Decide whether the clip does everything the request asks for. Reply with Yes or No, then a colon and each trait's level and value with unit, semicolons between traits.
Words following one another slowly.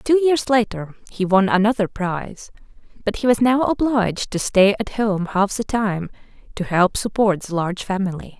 No: average, 180 wpm